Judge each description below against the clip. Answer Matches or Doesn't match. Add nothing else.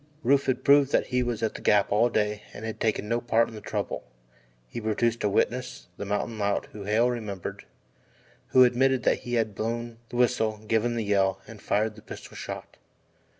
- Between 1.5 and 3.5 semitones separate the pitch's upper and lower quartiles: Matches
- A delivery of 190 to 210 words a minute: Matches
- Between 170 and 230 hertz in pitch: Doesn't match